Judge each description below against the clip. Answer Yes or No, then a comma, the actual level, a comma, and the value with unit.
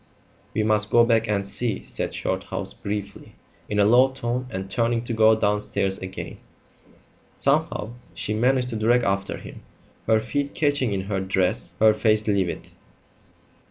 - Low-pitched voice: Yes, low, 110 Hz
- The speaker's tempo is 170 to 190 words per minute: No, average, 155 wpm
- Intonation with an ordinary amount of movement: Yes, average, 3.2 semitones